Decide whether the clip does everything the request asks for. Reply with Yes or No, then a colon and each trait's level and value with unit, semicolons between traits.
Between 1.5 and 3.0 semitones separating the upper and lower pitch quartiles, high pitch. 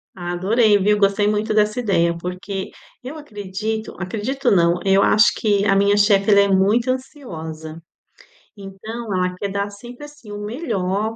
Yes: narrow, 2.6 semitones; high, 205 Hz